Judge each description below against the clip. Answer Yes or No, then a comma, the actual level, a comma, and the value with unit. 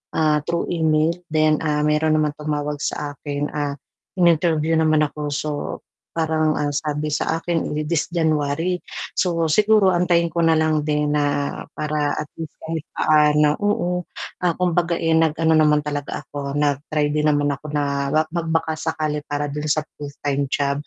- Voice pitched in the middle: Yes, medium, 155 Hz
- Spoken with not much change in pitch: Yes, narrow, 1.7 semitones